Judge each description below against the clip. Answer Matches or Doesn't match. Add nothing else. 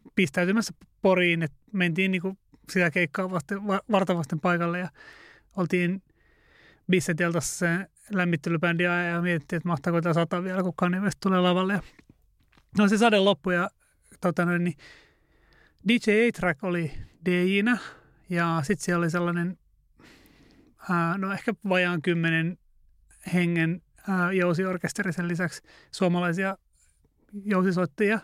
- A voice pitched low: Doesn't match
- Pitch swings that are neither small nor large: Doesn't match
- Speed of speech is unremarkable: Matches